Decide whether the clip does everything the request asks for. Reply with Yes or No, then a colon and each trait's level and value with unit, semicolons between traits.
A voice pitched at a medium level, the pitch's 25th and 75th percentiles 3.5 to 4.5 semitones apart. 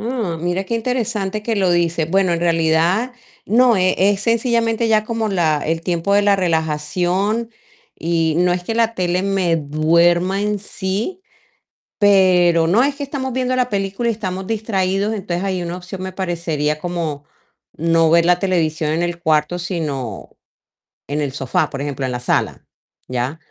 Yes: medium, 180 Hz; average, 4.1 semitones